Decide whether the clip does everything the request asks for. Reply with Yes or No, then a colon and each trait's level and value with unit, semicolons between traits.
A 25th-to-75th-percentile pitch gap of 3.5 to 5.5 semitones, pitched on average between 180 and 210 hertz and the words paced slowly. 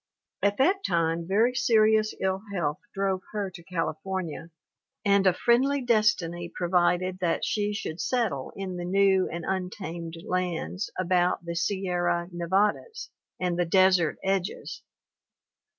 No: narrow, 2.6 semitones; medium, 185 Hz; slow, 130 wpm